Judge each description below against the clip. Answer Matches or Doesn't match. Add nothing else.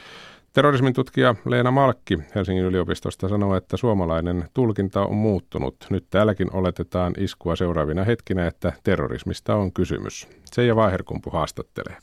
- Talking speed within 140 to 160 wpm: Doesn't match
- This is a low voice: Matches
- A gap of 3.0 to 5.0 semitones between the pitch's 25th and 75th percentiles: Matches